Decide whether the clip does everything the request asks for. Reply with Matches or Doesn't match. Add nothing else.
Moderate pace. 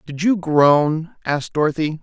Matches